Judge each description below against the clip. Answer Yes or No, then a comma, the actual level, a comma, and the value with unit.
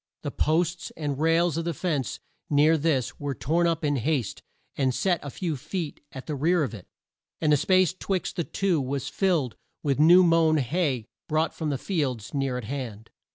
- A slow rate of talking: No, average, 195 wpm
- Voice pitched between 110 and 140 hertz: No, medium, 155 Hz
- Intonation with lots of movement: No, average, 3.8 semitones